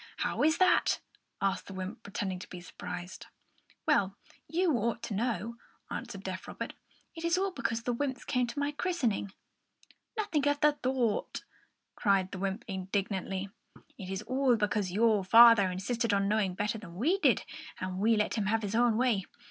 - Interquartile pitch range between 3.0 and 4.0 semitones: No, average, 4.8 semitones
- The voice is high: Yes, high, 220 Hz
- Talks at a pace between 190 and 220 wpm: No, average, 175 wpm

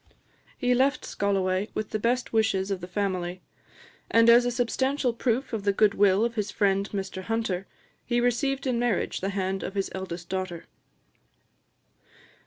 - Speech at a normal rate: Yes, average, 160 wpm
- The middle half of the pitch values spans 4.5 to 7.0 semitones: No, average, 3.9 semitones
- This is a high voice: Yes, high, 205 Hz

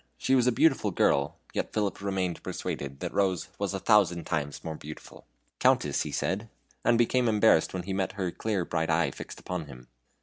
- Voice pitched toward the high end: No, very low, 95 Hz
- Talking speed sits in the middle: Yes, average, 195 wpm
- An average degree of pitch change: Yes, average, 4.7 semitones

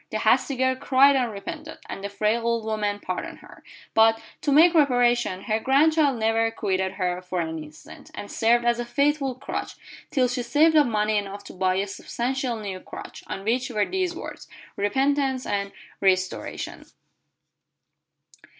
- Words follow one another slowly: No, average, 165 wpm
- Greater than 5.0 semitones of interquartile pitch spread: No, average, 4.7 semitones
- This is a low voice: No, high, 230 Hz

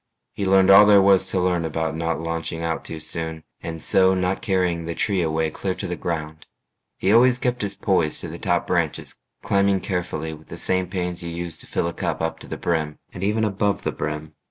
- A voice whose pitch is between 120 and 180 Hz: No, very low, 90 Hz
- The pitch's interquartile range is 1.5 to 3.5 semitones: Yes, average, 3.1 semitones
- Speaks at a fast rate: Yes, fast, 225 wpm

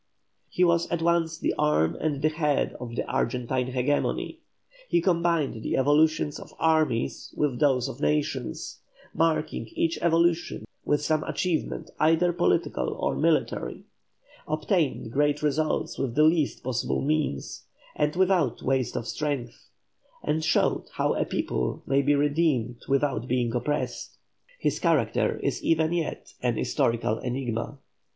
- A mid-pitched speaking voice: Yes, medium, 145 Hz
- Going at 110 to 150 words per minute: Yes, average, 140 wpm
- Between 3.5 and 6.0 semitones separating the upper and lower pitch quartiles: Yes, average, 4.3 semitones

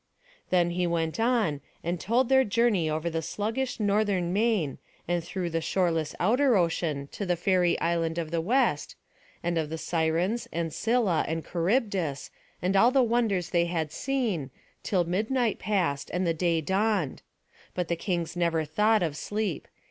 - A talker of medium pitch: Yes, medium, 175 Hz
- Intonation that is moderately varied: Yes, average, 4.6 semitones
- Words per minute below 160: No, average, 165 wpm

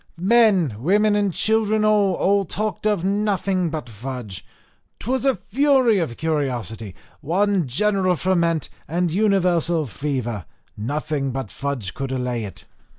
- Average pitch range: No, wide, 7.4 semitones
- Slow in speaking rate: Yes, slow, 130 wpm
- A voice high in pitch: No, medium, 170 Hz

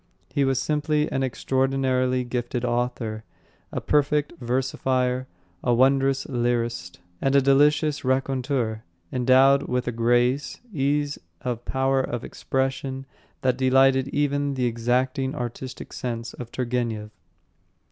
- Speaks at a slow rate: Yes, slow, 115 wpm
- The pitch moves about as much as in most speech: No, narrow, 1.8 semitones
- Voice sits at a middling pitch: No, low, 130 Hz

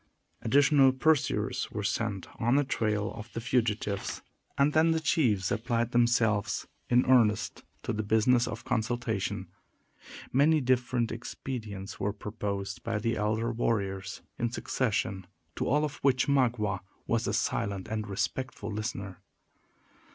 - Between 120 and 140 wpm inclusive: Yes, slow, 135 wpm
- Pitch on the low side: Yes, low, 115 Hz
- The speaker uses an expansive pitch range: No, average, 3.5 semitones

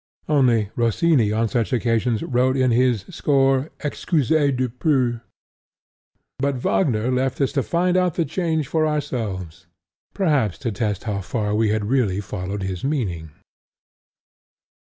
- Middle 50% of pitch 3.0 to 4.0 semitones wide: No, average, 5.1 semitones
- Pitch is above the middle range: No, low, 125 Hz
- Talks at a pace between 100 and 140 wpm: Yes, slow, 135 wpm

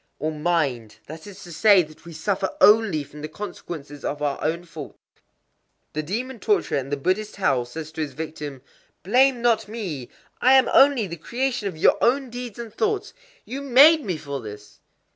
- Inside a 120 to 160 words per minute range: No, average, 175 wpm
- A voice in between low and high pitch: Yes, medium, 175 Hz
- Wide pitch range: Yes, wide, 7.7 semitones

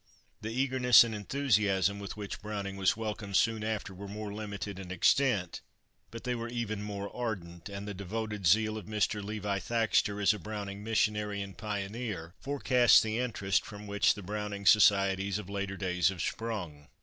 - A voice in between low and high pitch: No, low, 105 Hz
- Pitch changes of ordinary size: No, narrow, 1.9 semitones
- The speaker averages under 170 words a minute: No, average, 175 wpm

